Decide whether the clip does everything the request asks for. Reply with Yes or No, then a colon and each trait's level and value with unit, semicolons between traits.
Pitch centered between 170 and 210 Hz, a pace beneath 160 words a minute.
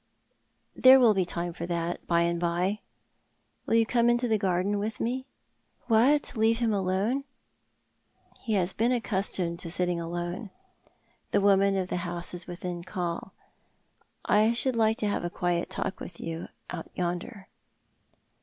No: high, 190 Hz; average, 175 wpm